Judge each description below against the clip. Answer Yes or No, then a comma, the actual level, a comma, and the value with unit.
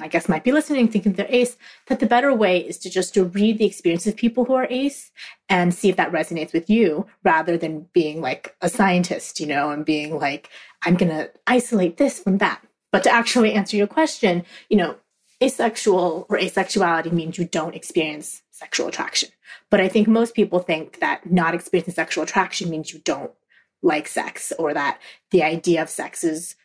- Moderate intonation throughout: Yes, average, 4.7 semitones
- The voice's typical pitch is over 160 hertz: Yes, medium, 185 Hz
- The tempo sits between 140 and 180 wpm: No, average, 200 wpm